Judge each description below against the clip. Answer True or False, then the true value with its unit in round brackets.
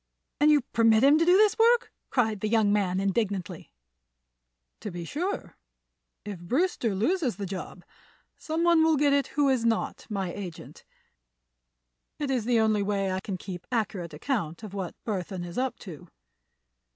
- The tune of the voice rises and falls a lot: True (6.8 semitones)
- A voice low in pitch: False (215 Hz)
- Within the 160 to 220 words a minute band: True (165 wpm)